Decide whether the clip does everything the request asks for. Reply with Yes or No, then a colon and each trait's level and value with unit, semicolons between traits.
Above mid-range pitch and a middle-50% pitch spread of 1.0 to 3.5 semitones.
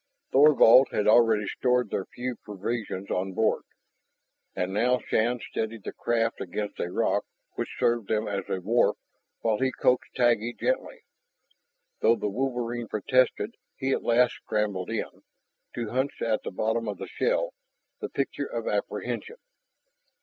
No: low, 115 Hz; average, 3.0 semitones